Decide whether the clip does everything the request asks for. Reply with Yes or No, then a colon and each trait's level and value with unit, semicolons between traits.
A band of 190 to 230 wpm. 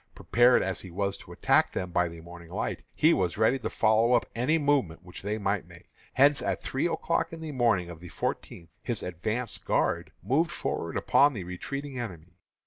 Yes: average, 200 wpm